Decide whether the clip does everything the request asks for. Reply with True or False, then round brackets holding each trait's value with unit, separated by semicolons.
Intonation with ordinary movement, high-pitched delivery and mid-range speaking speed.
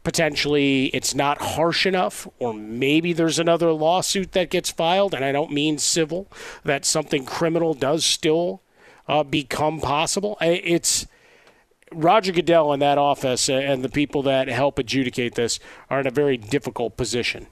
False (3.8 semitones; 145 Hz; 155 wpm)